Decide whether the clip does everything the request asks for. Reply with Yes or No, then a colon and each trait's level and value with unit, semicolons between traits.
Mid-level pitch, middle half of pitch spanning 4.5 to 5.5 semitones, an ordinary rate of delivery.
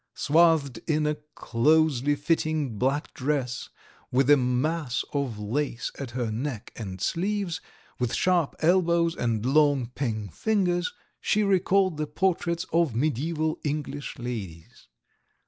No: medium, 145 Hz; average, 5.1 semitones; slow, 125 wpm